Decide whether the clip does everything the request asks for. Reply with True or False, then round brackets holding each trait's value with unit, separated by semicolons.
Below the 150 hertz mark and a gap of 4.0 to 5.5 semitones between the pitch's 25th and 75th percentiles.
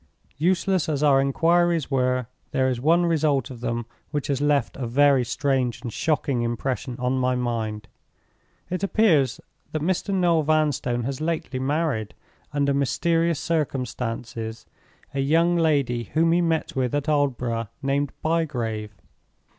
True (140 Hz; 4.4 semitones)